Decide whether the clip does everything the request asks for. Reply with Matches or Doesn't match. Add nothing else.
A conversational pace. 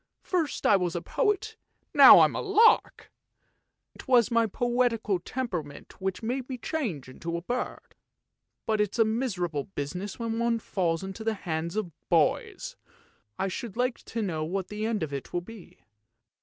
Matches